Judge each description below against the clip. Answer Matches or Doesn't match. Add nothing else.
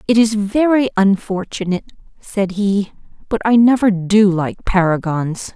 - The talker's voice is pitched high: Matches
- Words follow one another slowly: Matches